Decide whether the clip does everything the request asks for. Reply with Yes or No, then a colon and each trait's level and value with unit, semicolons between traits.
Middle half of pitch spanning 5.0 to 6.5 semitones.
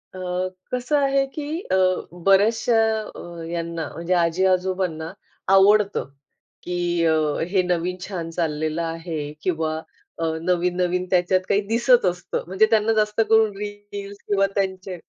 No: average, 3.3 semitones